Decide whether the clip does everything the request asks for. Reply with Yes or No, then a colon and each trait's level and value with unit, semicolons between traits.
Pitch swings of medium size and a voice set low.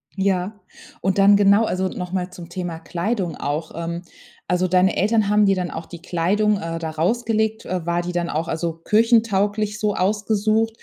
No: average, 3.5 semitones; high, 190 Hz